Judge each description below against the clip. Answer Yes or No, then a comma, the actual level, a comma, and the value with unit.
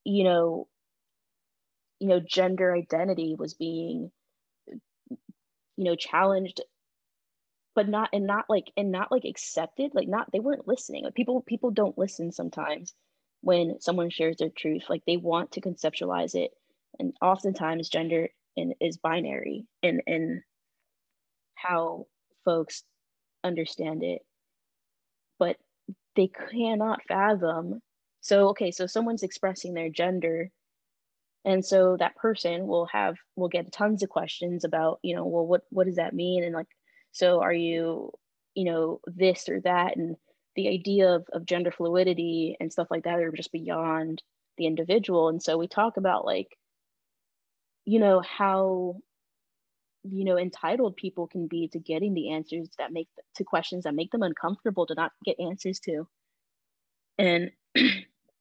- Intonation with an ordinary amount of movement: Yes, average, 3.2 semitones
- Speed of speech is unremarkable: Yes, average, 150 wpm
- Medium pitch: Yes, medium, 180 Hz